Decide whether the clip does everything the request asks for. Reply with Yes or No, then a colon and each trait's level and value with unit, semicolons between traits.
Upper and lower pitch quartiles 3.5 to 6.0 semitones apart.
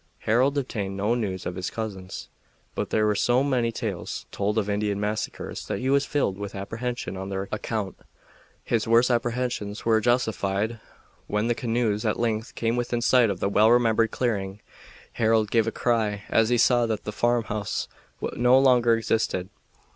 No: average, 2.7 semitones